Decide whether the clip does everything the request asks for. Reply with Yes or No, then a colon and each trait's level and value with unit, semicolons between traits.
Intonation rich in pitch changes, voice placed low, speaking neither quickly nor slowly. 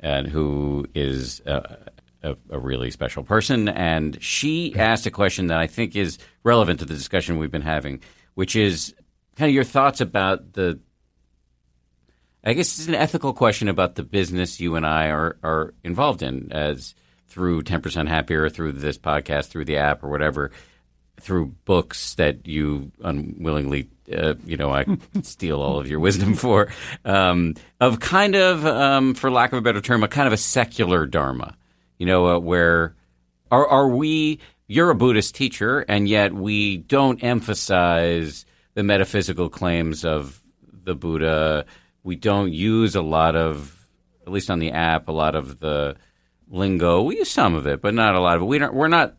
Yes: wide, 6.2 semitones; very low, 85 Hz; average, 180 wpm